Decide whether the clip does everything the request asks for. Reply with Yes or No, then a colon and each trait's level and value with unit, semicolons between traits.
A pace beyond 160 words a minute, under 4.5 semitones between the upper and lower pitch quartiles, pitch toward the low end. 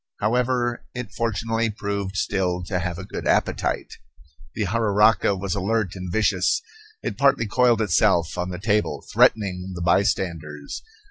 No: average, 140 wpm; average, 3.7 semitones; low, 100 Hz